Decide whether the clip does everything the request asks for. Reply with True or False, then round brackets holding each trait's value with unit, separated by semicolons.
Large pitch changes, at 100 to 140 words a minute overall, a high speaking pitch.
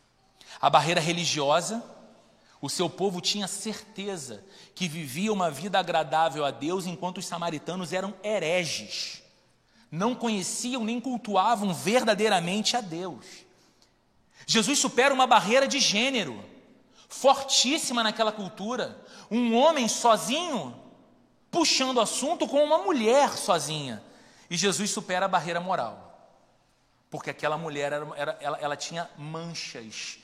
True (6.4 semitones; 120 wpm; 195 Hz)